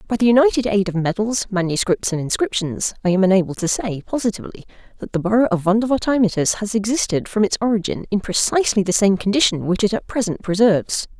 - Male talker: No, female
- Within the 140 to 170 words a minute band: No, average, 190 wpm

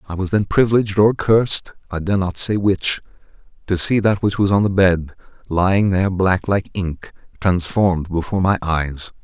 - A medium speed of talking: Yes, average, 180 wpm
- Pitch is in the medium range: No, very low, 95 Hz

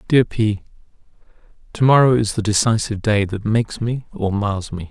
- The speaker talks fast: No, average, 170 wpm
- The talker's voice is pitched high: No, low, 110 Hz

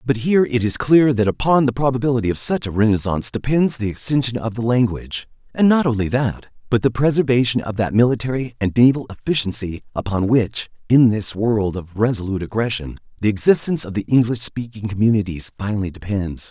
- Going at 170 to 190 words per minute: Yes, average, 180 wpm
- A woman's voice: No, male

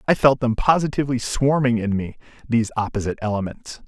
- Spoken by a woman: No, male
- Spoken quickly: No, average, 155 wpm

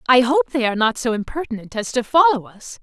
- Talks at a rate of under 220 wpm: No, fast, 235 wpm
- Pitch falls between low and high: No, very high, 250 Hz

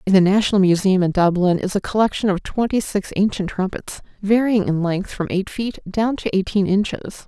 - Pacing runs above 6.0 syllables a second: No, 5.5 syllables/s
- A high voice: Yes, high, 195 Hz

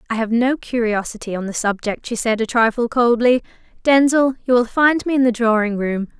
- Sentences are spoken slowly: No, fast, 205 wpm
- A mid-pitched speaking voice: No, high, 235 Hz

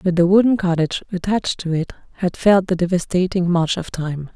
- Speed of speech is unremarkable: Yes, average, 195 wpm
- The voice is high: No, medium, 180 Hz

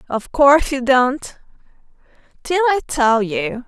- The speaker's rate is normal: No, slow, 115 wpm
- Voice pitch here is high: Yes, very high, 265 Hz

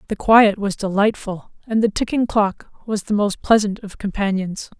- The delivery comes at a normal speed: Yes, average, 175 wpm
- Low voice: No, high, 205 Hz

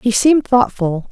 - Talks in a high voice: Yes, high, 225 Hz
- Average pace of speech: Yes, average, 160 wpm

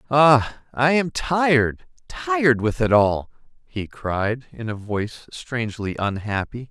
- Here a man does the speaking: Yes, male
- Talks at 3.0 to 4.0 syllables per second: Yes, 3.9 syllables/s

